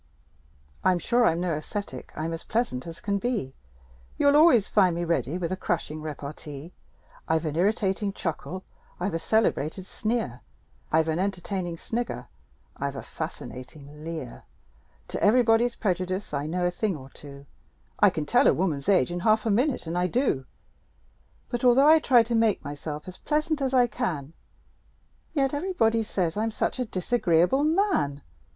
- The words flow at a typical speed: Yes, average, 165 wpm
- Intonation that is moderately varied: No, wide, 6.5 semitones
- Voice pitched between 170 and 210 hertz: Yes, medium, 185 Hz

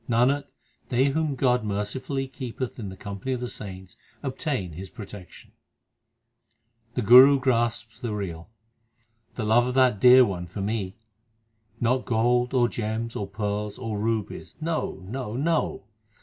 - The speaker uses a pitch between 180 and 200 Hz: No, low, 115 Hz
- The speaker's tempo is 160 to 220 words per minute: No, average, 150 wpm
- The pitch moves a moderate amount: Yes, average, 3.9 semitones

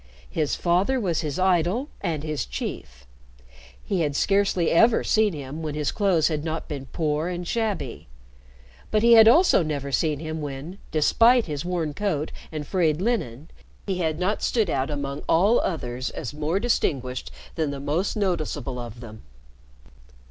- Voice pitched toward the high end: No, medium, 160 Hz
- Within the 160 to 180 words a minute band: Yes, average, 165 wpm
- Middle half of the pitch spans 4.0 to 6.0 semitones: Yes, average, 5.0 semitones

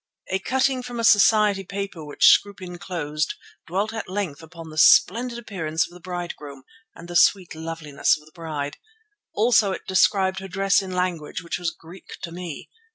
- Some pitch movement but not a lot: Yes, average, 3.6 semitones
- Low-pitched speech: No, medium, 180 Hz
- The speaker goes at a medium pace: Yes, average, 175 wpm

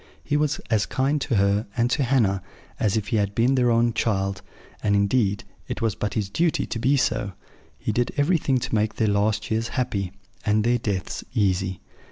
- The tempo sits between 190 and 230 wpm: Yes, average, 200 wpm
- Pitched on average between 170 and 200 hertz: No, low, 110 Hz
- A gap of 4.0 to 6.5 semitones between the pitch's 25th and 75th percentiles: No, average, 3.6 semitones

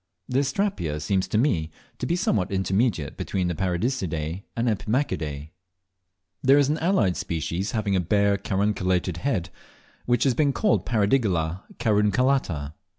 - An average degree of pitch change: No, wide, 6.3 semitones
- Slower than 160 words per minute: Yes, average, 140 wpm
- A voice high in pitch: No, low, 100 Hz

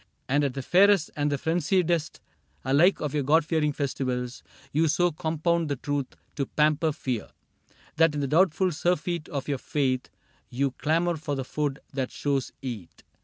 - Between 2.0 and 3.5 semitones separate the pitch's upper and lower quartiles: Yes, average, 3.0 semitones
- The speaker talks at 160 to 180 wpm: Yes, average, 170 wpm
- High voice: No, medium, 150 Hz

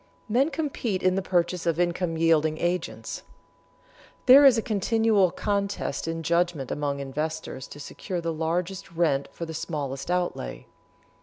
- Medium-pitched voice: Yes, medium, 170 Hz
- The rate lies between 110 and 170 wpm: Yes, average, 145 wpm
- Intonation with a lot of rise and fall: No, average, 3.4 semitones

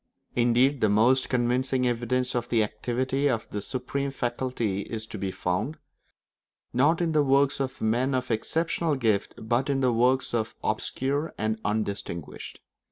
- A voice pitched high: No, low, 125 Hz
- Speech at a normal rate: Yes, average, 160 wpm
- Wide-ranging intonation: No, average, 3.4 semitones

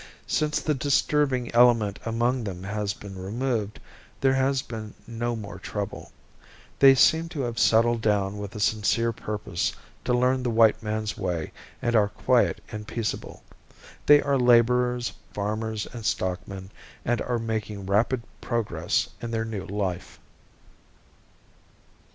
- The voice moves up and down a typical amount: Yes, average, 3.1 semitones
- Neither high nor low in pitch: No, low, 115 Hz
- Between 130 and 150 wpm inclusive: Yes, average, 140 wpm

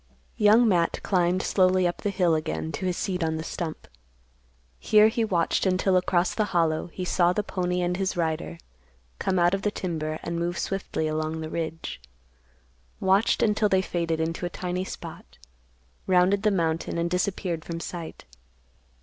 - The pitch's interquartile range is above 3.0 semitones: No, narrow, 2.4 semitones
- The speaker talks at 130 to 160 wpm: No, average, 170 wpm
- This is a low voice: No, medium, 180 Hz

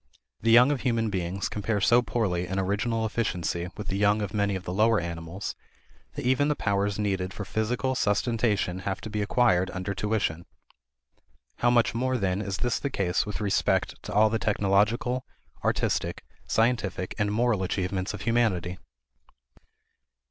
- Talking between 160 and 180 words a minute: Yes, average, 165 wpm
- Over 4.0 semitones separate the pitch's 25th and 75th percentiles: No, average, 3.4 semitones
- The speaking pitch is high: No, low, 105 Hz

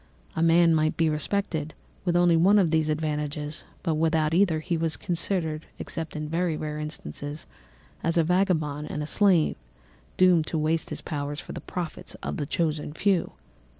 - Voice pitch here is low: No, medium, 160 Hz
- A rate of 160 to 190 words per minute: Yes, average, 175 wpm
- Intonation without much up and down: Yes, narrow, 2.2 semitones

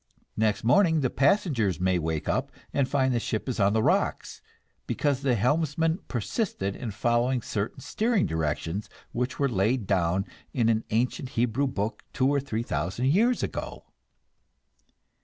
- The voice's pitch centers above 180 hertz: No, low, 120 Hz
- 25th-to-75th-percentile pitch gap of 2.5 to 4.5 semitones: No, wide, 5.6 semitones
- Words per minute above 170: No, average, 150 wpm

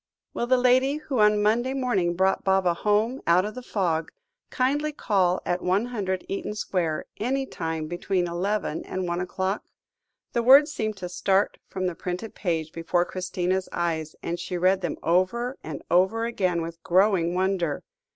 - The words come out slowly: No, average, 165 wpm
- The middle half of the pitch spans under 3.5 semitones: No, average, 4.2 semitones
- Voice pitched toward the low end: No, high, 190 Hz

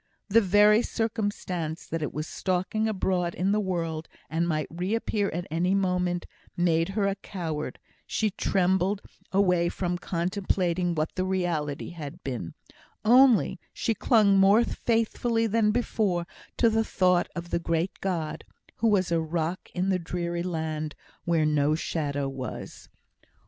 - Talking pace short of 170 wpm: Yes, average, 145 wpm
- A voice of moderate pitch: Yes, medium, 180 Hz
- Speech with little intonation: No, average, 3.5 semitones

